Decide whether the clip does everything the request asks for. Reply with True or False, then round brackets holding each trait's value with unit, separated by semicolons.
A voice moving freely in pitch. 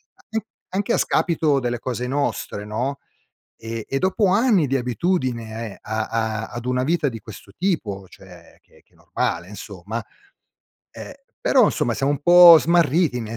True (7.2 semitones)